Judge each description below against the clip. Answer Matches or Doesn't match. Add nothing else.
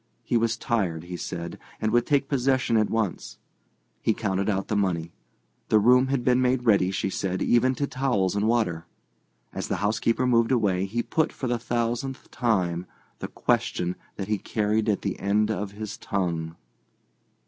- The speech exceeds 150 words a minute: Matches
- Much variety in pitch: Doesn't match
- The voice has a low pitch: Matches